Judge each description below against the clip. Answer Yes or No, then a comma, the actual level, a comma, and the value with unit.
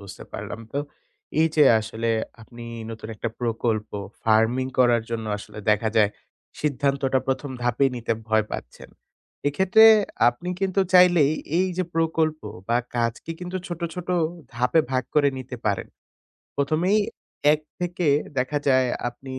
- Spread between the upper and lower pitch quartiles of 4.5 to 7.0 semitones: Yes, wide, 5.5 semitones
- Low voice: Yes, low, 130 Hz